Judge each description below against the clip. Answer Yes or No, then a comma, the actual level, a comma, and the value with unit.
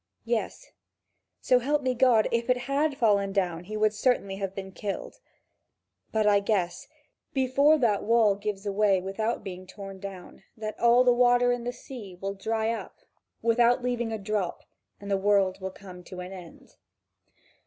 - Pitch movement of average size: Yes, average, 3.8 semitones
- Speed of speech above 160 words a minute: Yes, average, 170 wpm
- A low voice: No, high, 215 Hz